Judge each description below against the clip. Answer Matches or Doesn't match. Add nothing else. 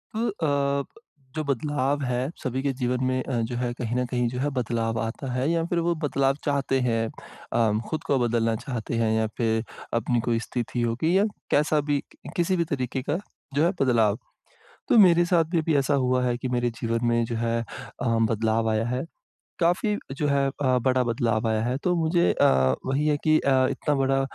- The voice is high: Doesn't match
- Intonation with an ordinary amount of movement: Matches